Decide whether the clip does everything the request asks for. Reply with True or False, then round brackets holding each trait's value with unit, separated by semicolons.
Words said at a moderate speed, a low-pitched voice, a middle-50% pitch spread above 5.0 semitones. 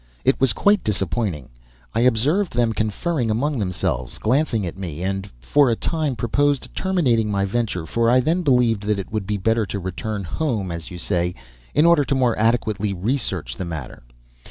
True (180 wpm; 110 Hz; 5.5 semitones)